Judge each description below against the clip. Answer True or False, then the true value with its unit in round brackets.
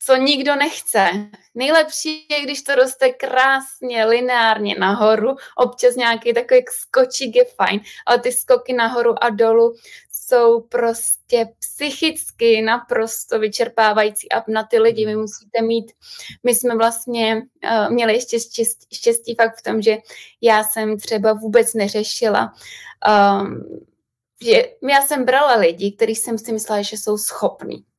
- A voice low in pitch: False (235 Hz)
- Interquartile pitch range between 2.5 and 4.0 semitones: True (2.9 semitones)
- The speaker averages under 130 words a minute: False (140 wpm)